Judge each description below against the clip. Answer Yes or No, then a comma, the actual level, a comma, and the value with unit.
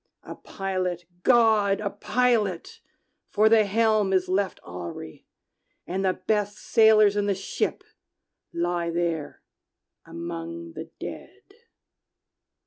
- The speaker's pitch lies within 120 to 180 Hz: No, high, 195 Hz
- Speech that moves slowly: Yes, slow, 110 wpm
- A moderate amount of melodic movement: Yes, average, 3.7 semitones